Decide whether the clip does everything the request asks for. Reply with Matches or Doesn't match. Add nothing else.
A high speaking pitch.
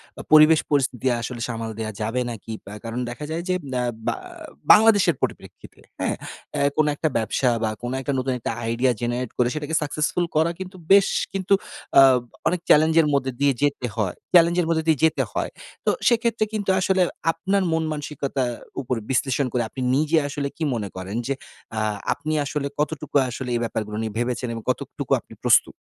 Doesn't match